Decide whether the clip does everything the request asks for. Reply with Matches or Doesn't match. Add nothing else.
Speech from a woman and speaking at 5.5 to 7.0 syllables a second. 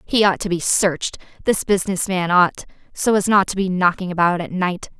Matches